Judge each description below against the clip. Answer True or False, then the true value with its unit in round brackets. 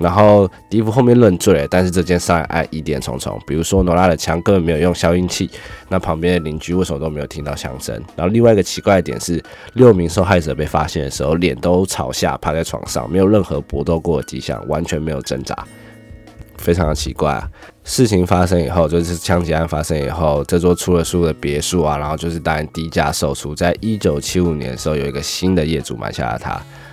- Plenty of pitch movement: False (2.9 semitones)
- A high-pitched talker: False (85 Hz)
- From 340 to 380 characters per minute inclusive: True (350 characters per minute)